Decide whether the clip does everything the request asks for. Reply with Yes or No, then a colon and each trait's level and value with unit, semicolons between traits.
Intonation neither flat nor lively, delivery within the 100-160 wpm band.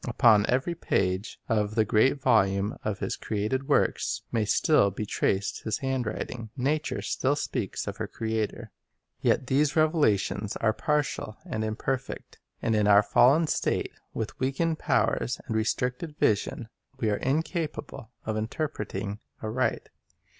Yes: average, 4.2 semitones; average, 140 wpm